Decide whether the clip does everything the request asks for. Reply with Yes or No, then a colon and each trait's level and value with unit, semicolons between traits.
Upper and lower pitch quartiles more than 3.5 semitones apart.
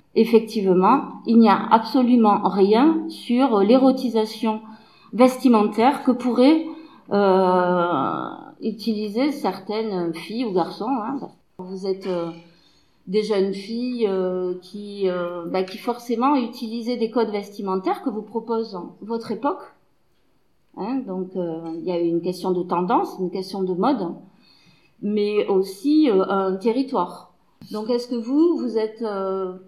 Yes: average, 4.7 semitones